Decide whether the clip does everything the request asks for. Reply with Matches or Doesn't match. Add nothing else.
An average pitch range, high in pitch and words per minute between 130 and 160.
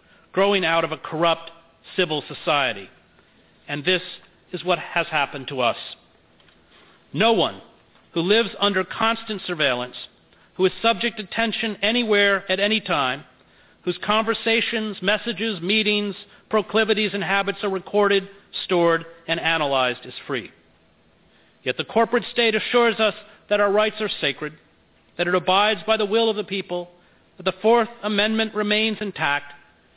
Matches